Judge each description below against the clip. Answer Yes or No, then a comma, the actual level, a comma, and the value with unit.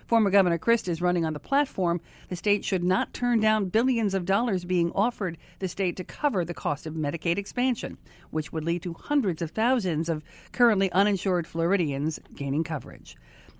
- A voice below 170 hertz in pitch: No, medium, 180 Hz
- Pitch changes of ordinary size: Yes, average, 4.2 semitones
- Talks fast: No, average, 180 wpm